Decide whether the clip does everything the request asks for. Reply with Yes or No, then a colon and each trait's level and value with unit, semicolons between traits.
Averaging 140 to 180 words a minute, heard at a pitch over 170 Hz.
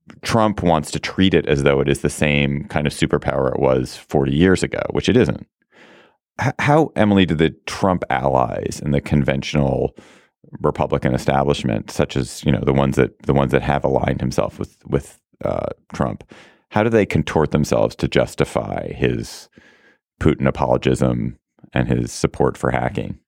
No: average, 170 wpm; very low, 70 Hz